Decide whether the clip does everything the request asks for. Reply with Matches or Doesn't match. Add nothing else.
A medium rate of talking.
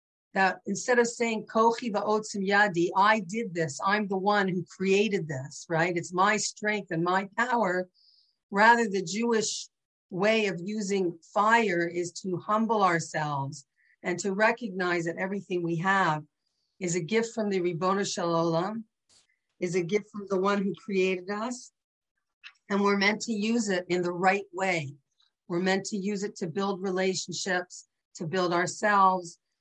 Matches